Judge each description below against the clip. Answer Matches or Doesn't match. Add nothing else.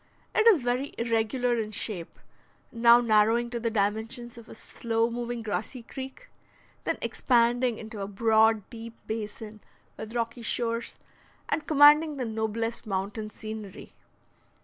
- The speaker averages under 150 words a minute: Matches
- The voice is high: Matches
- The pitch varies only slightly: Matches